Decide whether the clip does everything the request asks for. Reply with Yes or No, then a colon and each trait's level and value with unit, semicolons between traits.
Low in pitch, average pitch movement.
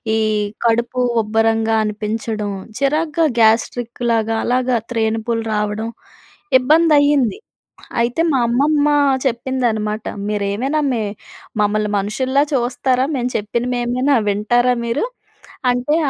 No: high, 235 Hz; average, 3.0 semitones